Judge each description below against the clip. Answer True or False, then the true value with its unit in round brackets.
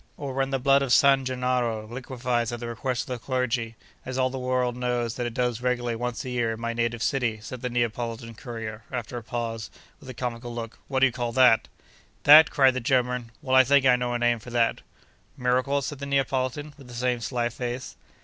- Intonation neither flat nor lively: False (1.7 semitones)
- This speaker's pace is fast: True (220 wpm)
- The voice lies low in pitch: True (125 Hz)